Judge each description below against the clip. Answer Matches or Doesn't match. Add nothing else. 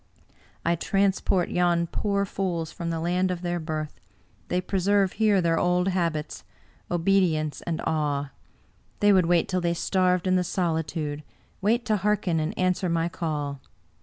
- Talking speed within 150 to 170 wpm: Matches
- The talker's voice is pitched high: Doesn't match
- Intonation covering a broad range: Doesn't match